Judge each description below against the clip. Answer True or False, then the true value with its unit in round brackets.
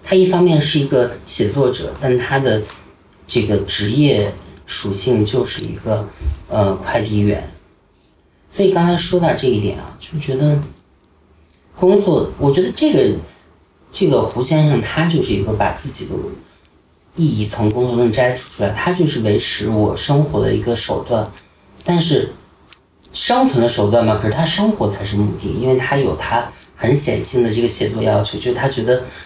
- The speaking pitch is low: True (120 Hz)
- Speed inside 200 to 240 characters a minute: False (250 characters per minute)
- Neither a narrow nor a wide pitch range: False (6.1 semitones)